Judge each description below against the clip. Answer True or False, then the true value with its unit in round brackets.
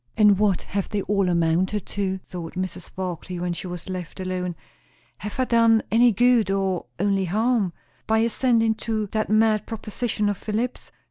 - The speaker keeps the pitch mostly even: False (3.2 semitones)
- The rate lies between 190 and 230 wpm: False (165 wpm)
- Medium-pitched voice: False (205 Hz)